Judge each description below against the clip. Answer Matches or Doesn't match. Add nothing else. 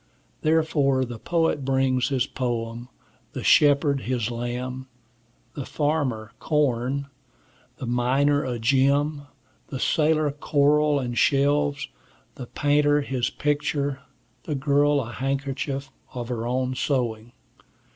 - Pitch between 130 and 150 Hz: Matches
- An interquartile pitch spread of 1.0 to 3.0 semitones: Matches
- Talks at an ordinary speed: Doesn't match